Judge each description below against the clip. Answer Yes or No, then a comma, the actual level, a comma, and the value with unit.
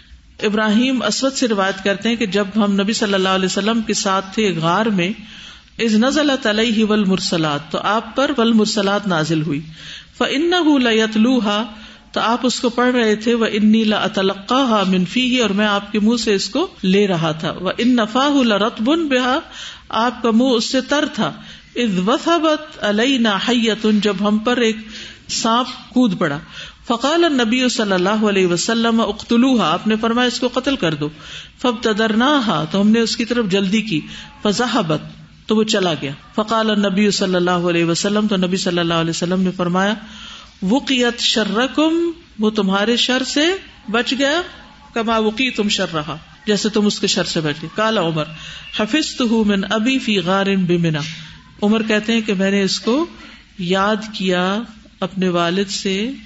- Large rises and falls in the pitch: No, average, 3.8 semitones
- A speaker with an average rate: Yes, average, 170 wpm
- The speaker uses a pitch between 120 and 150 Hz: No, high, 215 Hz